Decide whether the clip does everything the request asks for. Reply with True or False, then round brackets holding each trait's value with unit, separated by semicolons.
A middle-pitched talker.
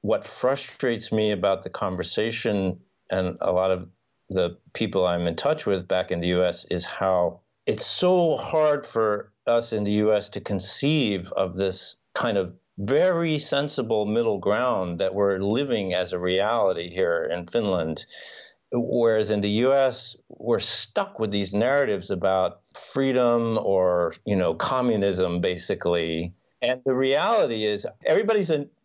False (110 Hz)